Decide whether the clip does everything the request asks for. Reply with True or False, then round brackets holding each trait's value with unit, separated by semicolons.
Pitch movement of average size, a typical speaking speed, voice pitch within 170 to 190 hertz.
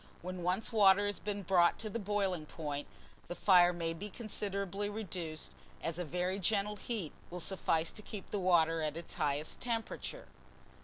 True (3.6 semitones; 170 wpm; 185 Hz)